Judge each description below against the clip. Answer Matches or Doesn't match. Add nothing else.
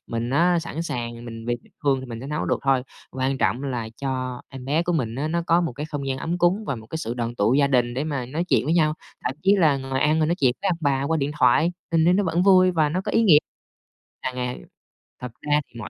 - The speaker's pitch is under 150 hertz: Matches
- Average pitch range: Matches